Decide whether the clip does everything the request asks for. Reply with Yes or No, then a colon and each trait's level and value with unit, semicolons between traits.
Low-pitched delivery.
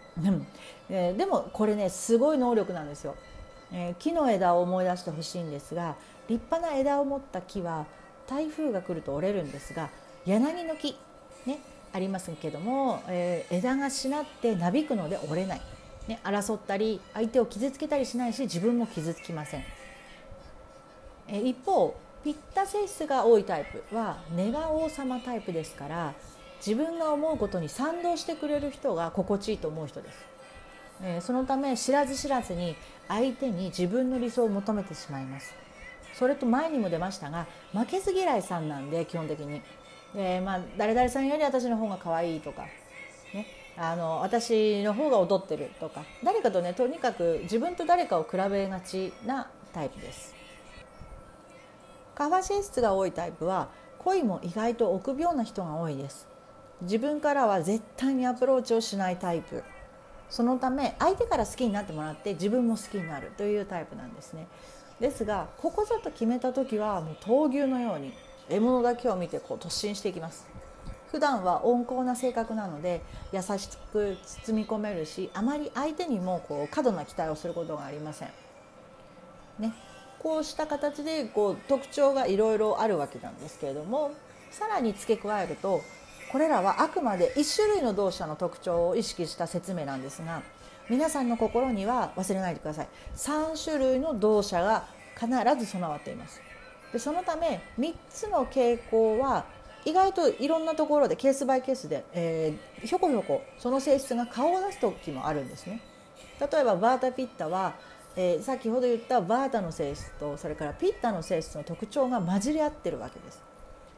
No: high, 230 Hz